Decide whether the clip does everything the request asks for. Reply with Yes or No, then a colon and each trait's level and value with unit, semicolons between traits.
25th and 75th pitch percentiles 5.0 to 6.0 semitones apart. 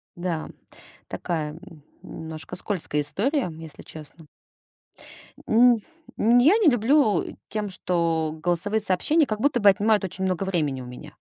Yes: wide, 5.4 semitones